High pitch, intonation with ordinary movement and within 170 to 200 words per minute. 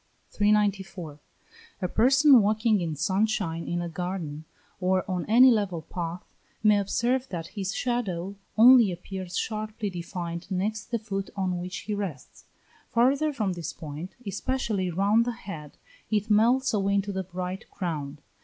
No: high, 195 Hz; average, 3.7 semitones; average, 150 wpm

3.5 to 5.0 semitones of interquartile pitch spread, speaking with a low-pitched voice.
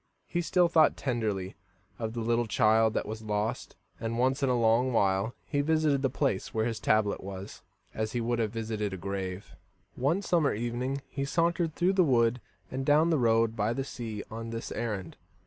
Yes: average, 4.1 semitones; low, 115 Hz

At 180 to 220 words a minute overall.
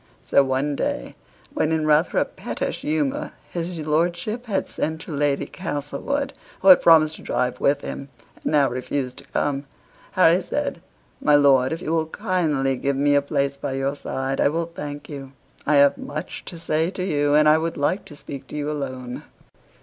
Yes: average, 190 wpm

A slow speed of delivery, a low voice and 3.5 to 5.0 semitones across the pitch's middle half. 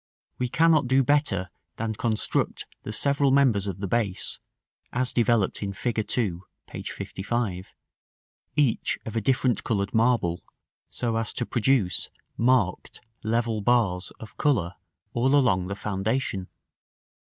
Yes: slow, 130 wpm; low, 115 Hz; average, 4.2 semitones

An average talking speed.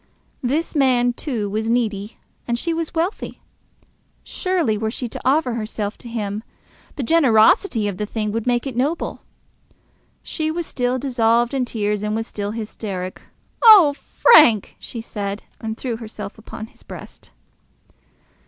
Yes: average, 150 wpm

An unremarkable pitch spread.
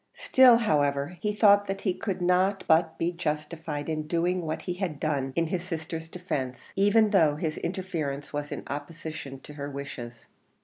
Yes: average, 3.9 semitones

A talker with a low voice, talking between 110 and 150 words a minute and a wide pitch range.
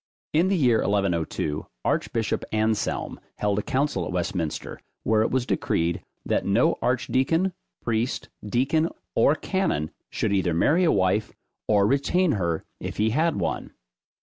Yes: low, 110 Hz; average, 140 wpm; wide, 6.7 semitones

